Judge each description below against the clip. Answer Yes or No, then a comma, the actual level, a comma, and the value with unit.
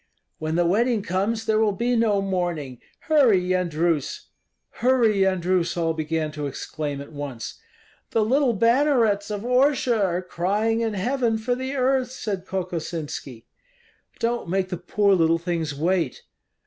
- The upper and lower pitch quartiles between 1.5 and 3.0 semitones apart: No, wide, 5.6 semitones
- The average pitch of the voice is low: No, high, 190 Hz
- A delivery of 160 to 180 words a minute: No, average, 145 wpm